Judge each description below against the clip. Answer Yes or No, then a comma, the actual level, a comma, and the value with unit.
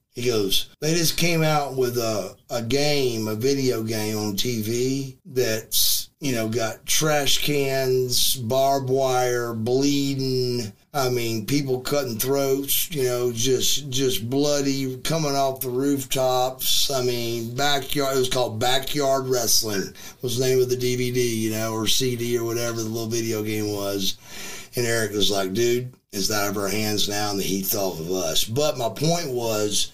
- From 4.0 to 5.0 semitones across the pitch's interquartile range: No, average, 3.3 semitones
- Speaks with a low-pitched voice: Yes, low, 125 Hz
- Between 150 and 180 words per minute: Yes, average, 170 wpm